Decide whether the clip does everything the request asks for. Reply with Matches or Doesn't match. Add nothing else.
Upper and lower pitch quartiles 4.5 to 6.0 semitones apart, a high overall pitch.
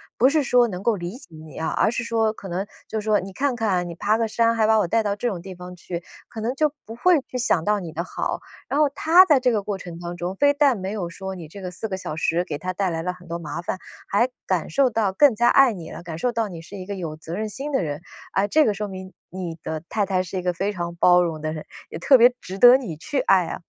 Matches